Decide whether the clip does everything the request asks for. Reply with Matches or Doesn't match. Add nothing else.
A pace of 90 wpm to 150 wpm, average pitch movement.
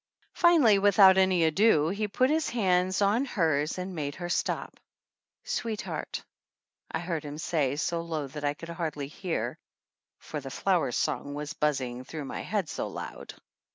Doesn't match